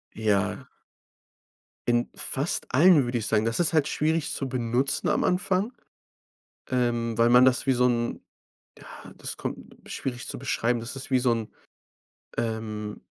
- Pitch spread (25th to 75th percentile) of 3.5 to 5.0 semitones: No, average, 2.8 semitones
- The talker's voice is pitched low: Yes, low, 125 Hz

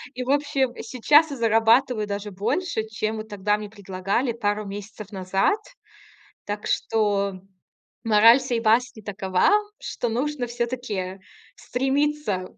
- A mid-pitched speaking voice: No, high, 220 Hz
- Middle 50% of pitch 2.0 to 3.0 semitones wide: No, average, 3.6 semitones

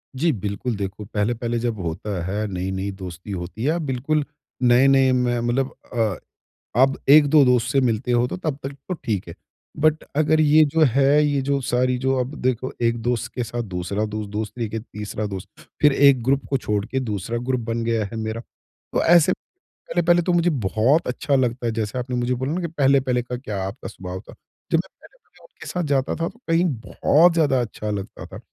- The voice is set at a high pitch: No, low, 125 Hz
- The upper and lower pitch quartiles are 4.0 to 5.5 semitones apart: Yes, average, 4.6 semitones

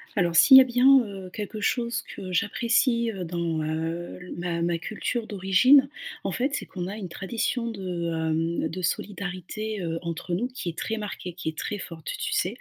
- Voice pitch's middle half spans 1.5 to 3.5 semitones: No, average, 5.0 semitones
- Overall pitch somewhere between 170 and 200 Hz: Yes, medium, 185 Hz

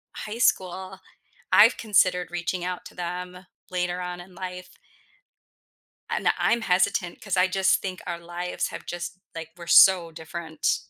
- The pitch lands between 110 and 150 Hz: No, medium, 180 Hz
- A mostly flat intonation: Yes, narrow, 1.3 semitones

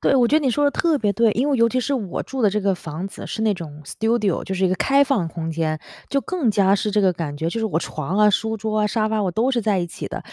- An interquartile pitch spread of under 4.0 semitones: No, average, 4.7 semitones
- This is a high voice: Yes, high, 210 Hz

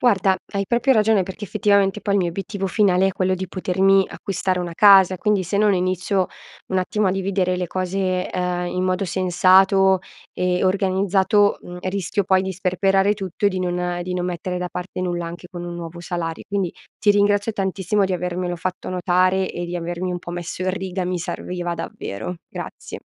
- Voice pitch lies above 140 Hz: Yes, medium, 185 Hz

